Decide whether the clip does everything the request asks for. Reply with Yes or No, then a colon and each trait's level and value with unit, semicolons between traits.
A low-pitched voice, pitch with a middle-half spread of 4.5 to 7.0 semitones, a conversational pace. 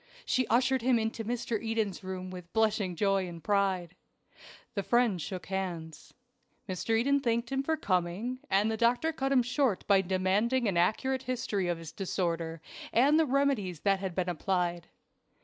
No: high, 205 Hz; average, 5.0 semitones; average, 165 wpm